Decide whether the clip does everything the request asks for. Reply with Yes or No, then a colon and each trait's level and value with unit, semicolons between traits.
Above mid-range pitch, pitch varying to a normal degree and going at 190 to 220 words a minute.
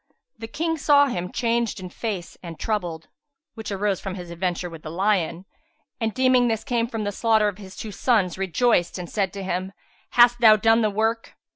Yes: high, 210 Hz; average, 3.9 semitones; average, 195 wpm